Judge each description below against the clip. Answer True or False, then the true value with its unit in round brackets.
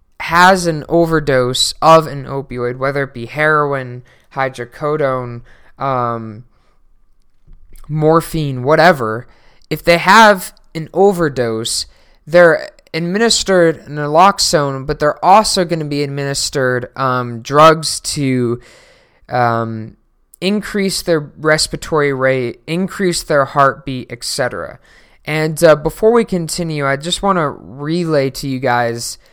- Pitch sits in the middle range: True (145 Hz)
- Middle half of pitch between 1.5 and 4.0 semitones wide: False (4.8 semitones)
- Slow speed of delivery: True (110 wpm)